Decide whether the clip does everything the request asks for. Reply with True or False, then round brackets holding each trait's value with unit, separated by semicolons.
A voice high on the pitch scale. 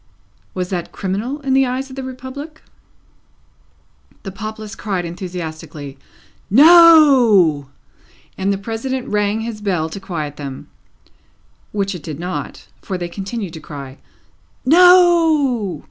True (205 Hz)